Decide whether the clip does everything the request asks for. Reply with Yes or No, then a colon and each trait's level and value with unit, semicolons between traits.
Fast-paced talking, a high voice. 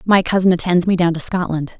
No: fast, 235 wpm; medium, 175 Hz